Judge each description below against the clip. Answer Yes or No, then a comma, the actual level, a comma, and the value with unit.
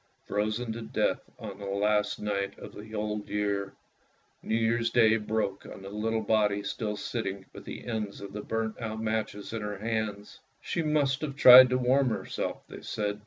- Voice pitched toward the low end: Yes, low, 110 Hz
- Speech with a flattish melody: Yes, narrow, 1.7 semitones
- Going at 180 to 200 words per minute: Yes, average, 185 wpm